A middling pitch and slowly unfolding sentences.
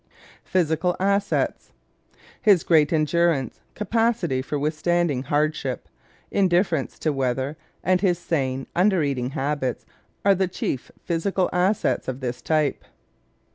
Yes: medium, 160 Hz; slow, 120 wpm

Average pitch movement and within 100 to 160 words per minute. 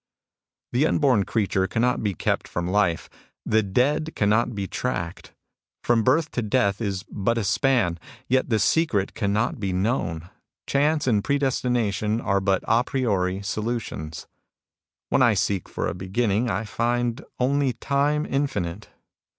Yes: average, 4.4 semitones; average, 150 wpm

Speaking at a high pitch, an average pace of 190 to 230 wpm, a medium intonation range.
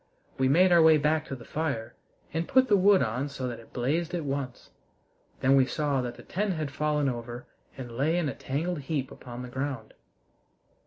No: medium, 140 Hz; fast, 205 wpm; average, 4.0 semitones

